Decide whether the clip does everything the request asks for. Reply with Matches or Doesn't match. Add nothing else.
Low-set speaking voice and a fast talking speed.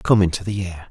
Matches